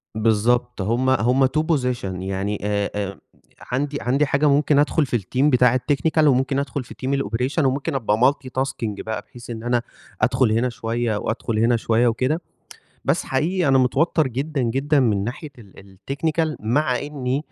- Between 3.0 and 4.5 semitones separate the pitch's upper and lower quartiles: Yes, average, 3.7 semitones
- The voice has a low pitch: Yes, low, 125 Hz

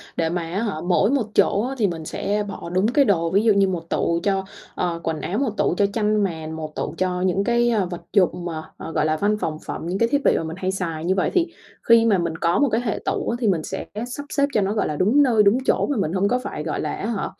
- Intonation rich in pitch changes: No, average, 4.7 semitones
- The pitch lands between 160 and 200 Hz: Yes, high, 195 Hz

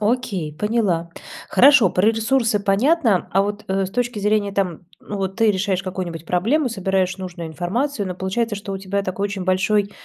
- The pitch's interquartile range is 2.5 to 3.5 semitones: Yes, average, 2.9 semitones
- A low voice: No, high, 195 Hz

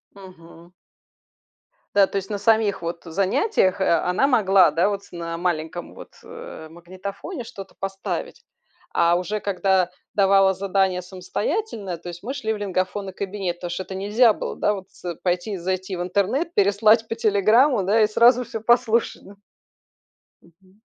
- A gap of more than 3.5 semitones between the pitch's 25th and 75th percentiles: No, average, 3.0 semitones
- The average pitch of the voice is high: Yes, high, 195 Hz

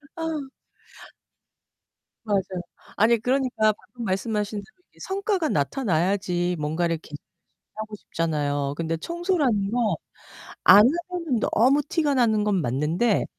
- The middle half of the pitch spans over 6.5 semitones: Yes, wide, 7.4 semitones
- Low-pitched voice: No, high, 215 Hz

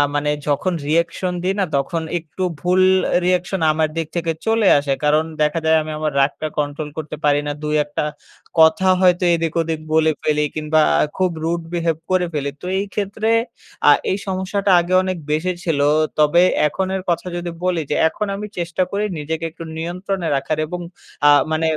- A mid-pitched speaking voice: Yes, medium, 165 Hz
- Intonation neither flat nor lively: Yes, average, 3.1 semitones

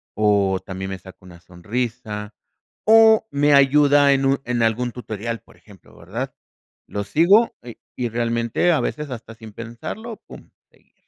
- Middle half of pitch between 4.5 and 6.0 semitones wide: Yes, average, 5.1 semitones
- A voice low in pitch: Yes, low, 115 Hz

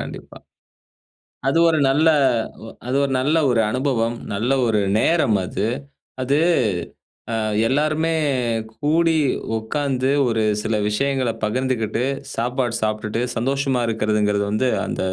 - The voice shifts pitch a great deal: No, average, 4.0 semitones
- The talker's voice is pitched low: Yes, low, 125 Hz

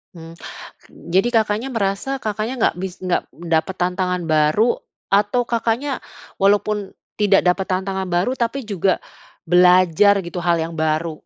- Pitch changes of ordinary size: Yes, average, 3.6 semitones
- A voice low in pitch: No, high, 190 Hz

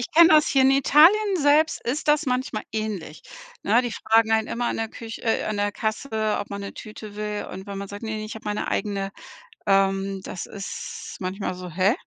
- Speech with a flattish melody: No, average, 3.4 semitones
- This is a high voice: Yes, high, 215 Hz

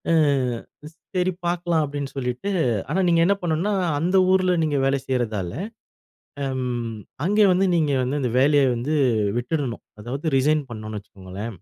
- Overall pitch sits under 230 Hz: Yes, medium, 140 Hz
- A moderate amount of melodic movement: No, wide, 5.7 semitones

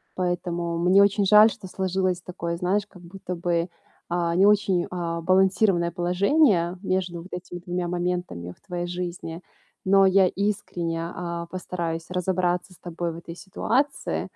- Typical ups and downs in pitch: No, narrow, 1.7 semitones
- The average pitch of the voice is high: No, medium, 180 Hz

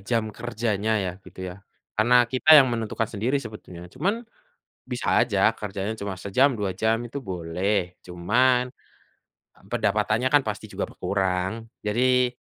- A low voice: Yes, low, 110 Hz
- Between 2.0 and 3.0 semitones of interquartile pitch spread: No, average, 4.2 semitones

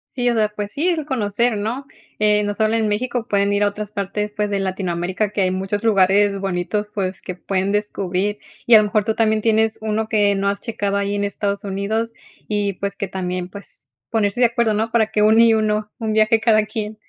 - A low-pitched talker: No, high, 210 Hz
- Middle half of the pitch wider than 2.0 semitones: No, narrow, 1.7 semitones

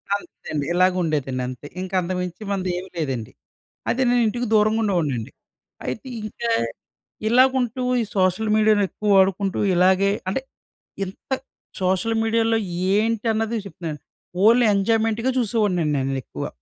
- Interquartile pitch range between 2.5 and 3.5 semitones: No, average, 4.0 semitones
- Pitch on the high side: Yes, high, 200 Hz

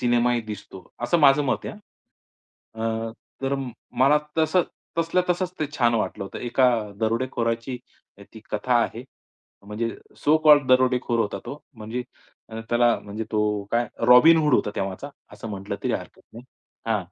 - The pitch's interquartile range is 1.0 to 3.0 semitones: No, average, 3.6 semitones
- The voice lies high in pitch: No, low, 120 Hz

